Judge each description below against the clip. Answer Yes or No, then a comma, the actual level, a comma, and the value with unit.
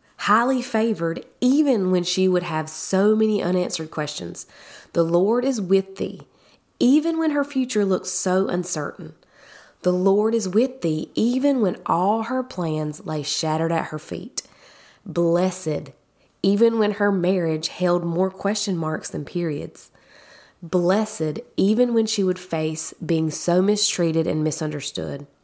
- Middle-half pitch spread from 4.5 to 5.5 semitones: Yes, average, 4.8 semitones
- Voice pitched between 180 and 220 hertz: Yes, medium, 185 Hz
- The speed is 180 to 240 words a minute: No, average, 140 wpm